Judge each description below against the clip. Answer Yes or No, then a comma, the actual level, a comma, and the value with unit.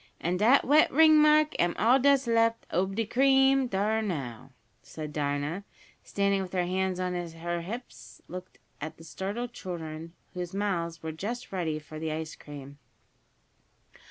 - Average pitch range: No, wide, 5.9 semitones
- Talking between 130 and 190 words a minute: Yes, average, 155 wpm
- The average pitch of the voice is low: No, medium, 185 Hz